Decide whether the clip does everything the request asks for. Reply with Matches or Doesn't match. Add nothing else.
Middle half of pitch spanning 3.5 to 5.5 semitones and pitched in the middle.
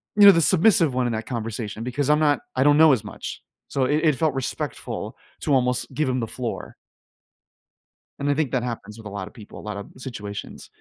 Doesn't match